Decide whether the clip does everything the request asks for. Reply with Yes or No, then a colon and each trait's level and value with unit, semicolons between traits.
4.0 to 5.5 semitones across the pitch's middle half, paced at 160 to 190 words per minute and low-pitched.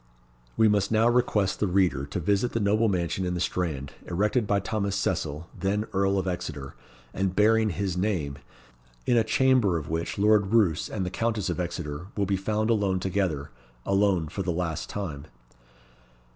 No: average, 3.3 semitones; average, 175 wpm; very low, 95 Hz